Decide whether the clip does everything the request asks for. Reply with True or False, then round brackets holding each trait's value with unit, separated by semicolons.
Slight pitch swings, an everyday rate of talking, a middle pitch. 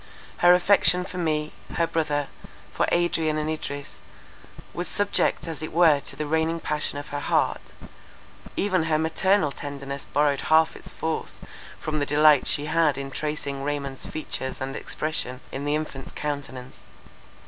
True (2.2 semitones; 155 wpm; 150 Hz)